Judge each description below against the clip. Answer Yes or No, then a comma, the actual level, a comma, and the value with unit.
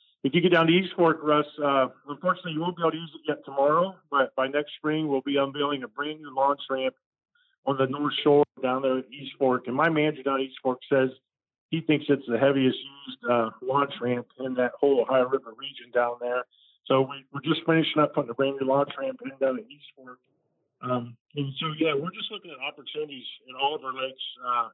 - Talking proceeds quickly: Yes, fast, 235 wpm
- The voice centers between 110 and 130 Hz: No, medium, 140 Hz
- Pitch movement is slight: No, average, 3.1 semitones